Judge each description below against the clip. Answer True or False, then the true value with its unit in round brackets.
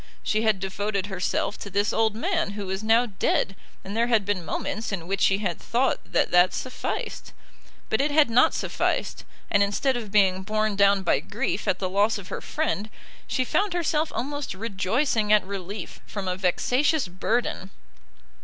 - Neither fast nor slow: True (180 wpm)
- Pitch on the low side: False (205 Hz)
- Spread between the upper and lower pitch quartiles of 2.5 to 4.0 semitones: True (3.7 semitones)